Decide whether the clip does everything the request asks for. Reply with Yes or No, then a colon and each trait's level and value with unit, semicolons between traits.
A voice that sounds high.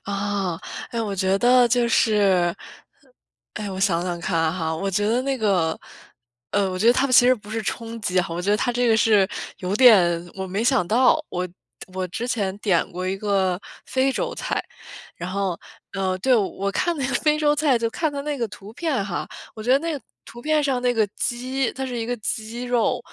Yes: high, 215 Hz